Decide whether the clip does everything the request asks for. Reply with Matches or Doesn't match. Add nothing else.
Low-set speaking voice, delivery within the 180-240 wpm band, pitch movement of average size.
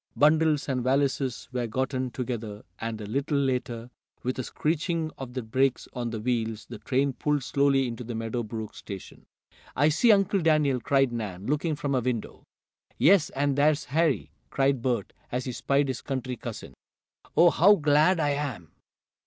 Doesn't match